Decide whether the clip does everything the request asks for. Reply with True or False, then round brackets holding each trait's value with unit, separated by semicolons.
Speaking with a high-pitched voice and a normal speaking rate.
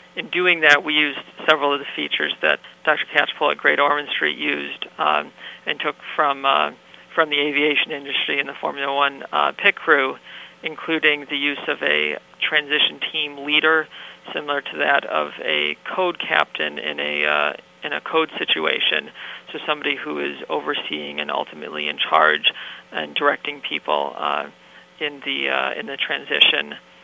False (140 Hz; 165 wpm)